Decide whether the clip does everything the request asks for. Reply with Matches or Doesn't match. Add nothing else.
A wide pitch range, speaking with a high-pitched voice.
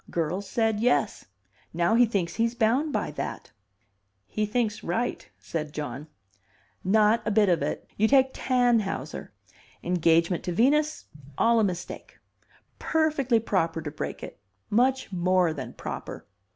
Matches